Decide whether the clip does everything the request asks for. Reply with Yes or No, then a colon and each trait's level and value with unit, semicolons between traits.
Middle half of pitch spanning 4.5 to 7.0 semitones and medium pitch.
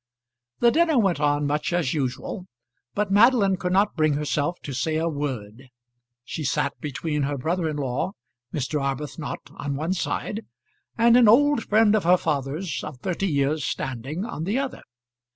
Yes: wide, 5.6 semitones; medium, 155 Hz